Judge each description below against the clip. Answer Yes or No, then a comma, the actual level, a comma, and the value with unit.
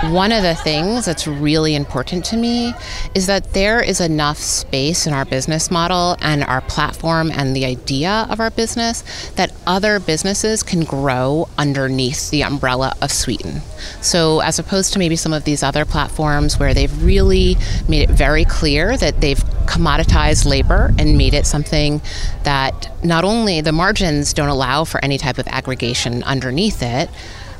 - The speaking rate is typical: Yes, average, 165 wpm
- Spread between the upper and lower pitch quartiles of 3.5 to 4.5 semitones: No, average, 4.9 semitones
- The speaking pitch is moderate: Yes, medium, 150 Hz